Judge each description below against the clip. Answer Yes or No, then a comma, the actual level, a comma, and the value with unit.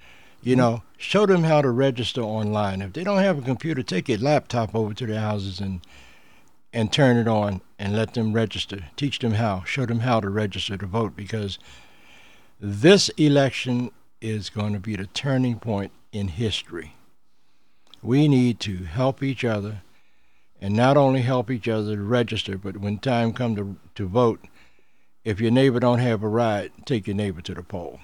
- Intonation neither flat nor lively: Yes, average, 3.8 semitones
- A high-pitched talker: No, low, 110 Hz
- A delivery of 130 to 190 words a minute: Yes, average, 185 wpm